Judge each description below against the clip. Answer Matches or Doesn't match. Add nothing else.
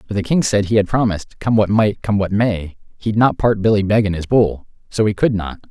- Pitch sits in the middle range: Doesn't match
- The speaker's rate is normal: Doesn't match